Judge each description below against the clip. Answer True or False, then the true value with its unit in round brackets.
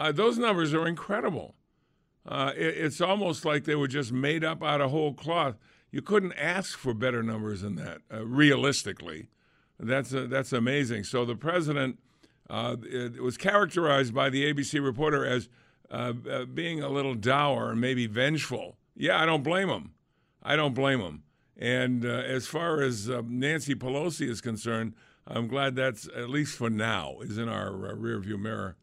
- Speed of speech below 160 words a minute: False (180 wpm)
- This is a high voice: False (135 Hz)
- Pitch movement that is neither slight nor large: True (4.3 semitones)